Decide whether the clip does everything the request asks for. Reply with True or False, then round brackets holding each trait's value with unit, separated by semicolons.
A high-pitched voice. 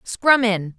True (215 Hz)